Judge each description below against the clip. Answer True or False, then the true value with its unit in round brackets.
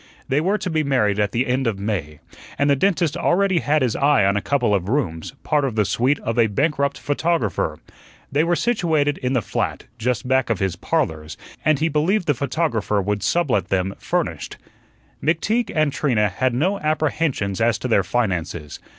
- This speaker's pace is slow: False (190 wpm)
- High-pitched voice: False (130 Hz)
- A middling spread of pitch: False (7.0 semitones)